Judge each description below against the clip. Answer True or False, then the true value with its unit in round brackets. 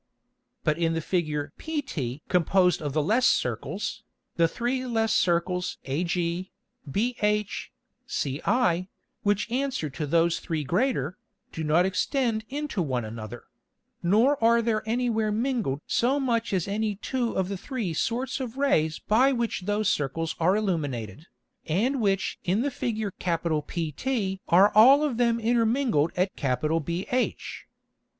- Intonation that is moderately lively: False (6.3 semitones)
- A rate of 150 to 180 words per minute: False (140 wpm)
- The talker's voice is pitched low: False (195 Hz)